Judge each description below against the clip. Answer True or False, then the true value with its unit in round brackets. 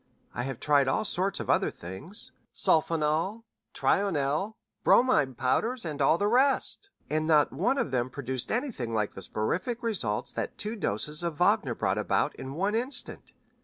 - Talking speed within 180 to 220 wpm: False (165 wpm)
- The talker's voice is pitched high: False (155 Hz)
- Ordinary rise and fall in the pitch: False (8.5 semitones)